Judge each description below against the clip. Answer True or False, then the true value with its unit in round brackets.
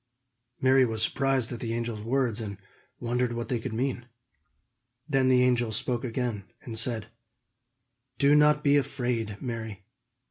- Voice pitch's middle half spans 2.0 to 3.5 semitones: True (2.6 semitones)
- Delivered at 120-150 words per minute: True (145 wpm)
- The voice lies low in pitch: True (120 Hz)